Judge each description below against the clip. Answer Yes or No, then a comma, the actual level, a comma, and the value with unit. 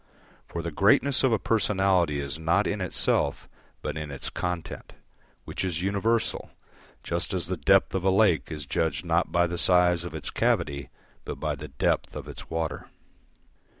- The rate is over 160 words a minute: Yes, average, 175 wpm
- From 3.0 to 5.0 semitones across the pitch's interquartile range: Yes, average, 3.8 semitones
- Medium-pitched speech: No, very low, 85 Hz